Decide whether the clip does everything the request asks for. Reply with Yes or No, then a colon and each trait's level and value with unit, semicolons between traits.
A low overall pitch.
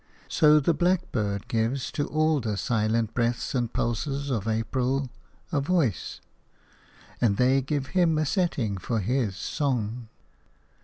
Yes: low, 125 Hz